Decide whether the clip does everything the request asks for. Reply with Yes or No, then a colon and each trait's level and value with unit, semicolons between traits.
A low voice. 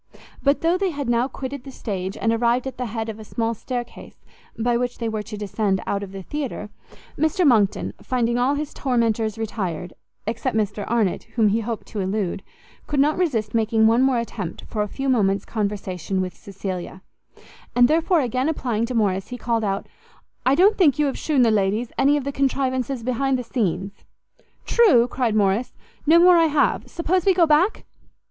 No: high, 235 Hz